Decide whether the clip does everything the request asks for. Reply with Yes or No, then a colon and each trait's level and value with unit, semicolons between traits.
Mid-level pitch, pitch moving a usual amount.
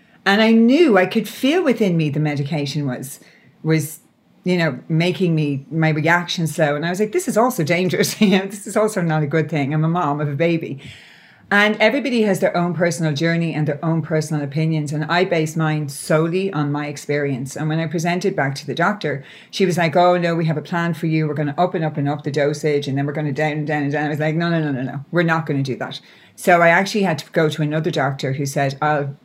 Yes: medium, 160 Hz; average, 3.1 semitones